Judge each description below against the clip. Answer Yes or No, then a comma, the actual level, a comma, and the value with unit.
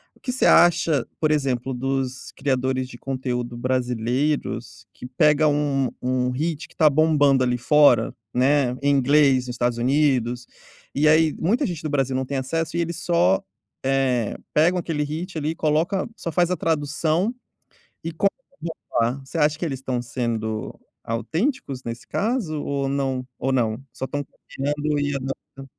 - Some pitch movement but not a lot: Yes, average, 3.6 semitones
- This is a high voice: No, medium, 140 Hz